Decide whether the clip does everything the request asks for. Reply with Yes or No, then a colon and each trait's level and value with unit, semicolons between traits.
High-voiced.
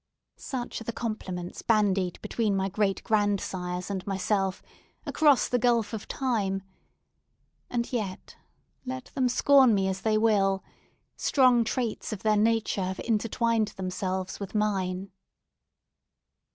Yes: high, 210 Hz